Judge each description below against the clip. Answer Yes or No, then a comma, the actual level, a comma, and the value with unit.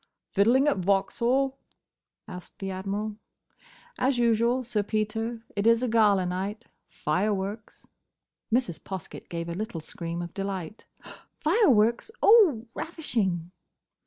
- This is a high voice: Yes, high, 215 Hz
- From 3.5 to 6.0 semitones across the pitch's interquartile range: Yes, average, 3.9 semitones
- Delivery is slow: Yes, slow, 115 wpm